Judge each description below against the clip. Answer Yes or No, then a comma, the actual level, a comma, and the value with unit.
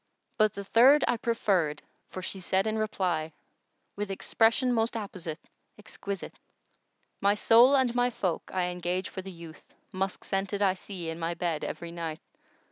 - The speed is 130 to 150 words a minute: No, average, 170 wpm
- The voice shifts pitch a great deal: No, average, 4.0 semitones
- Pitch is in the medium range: No, high, 195 Hz